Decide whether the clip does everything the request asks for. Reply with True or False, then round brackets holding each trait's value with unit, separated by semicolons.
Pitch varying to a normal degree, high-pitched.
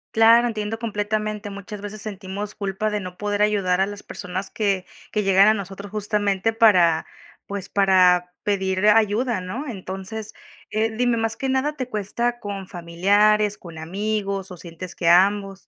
False (2.2 semitones; 205 Hz)